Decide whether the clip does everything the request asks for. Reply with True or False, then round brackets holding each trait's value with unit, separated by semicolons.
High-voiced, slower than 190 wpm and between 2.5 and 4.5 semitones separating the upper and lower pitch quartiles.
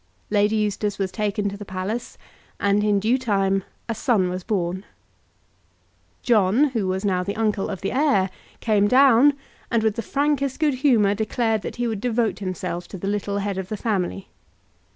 True (210 Hz; 180 wpm; 3.1 semitones)